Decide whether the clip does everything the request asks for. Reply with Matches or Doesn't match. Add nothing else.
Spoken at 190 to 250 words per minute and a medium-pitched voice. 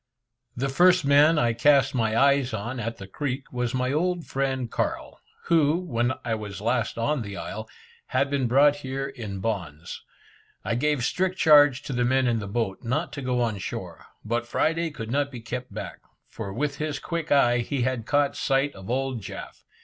Doesn't match